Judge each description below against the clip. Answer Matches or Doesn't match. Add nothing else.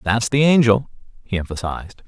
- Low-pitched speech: Matches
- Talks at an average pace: Matches